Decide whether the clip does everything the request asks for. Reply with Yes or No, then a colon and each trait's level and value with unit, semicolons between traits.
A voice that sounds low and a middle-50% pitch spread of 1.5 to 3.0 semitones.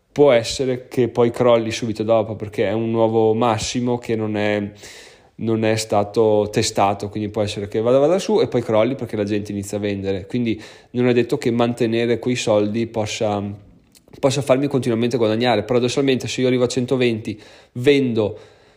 Yes: low, 115 Hz; average, 2.7 semitones